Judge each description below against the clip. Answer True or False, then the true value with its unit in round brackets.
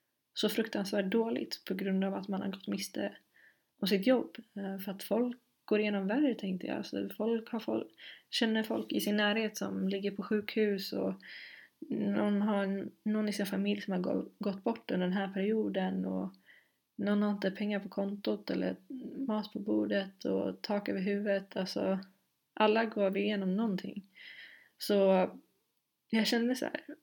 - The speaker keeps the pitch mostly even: True (2.2 semitones)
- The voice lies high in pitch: True (205 Hz)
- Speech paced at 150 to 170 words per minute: True (165 wpm)